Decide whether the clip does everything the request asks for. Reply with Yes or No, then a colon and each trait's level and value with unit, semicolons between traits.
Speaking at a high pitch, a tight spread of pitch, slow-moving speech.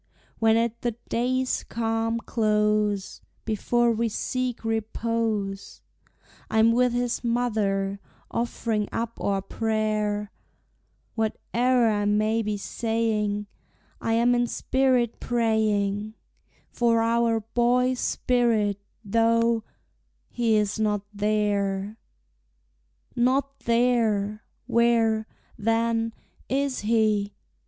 Yes: high, 225 Hz; narrow, 1.9 semitones; slow, 95 wpm